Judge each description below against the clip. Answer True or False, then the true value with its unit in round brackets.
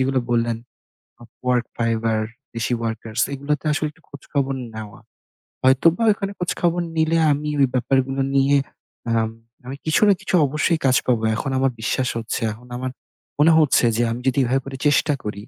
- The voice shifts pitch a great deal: False (4.0 semitones)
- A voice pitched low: True (130 Hz)